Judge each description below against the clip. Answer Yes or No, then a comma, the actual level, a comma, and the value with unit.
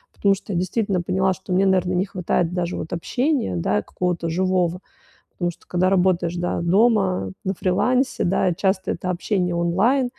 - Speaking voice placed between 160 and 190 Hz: Yes, medium, 185 Hz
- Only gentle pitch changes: Yes, narrow, 1.9 semitones